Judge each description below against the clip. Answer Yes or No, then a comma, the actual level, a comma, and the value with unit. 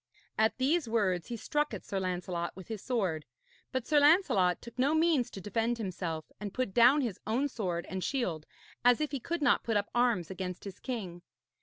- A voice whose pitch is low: No, high, 225 Hz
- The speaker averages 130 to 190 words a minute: No, average, 200 wpm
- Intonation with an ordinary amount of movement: No, wide, 5.8 semitones